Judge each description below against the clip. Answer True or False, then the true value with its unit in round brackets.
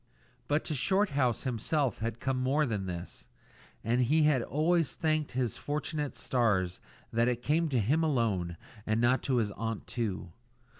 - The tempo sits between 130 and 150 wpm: False (160 wpm)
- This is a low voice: True (125 Hz)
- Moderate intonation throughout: True (4.9 semitones)